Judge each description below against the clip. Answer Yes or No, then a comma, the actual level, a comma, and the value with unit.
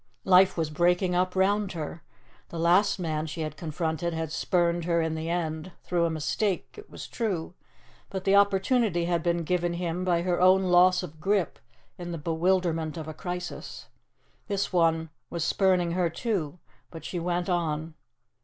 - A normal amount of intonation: No, narrow, 2.3 semitones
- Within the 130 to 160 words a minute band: No, average, 170 wpm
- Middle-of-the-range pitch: Yes, medium, 175 Hz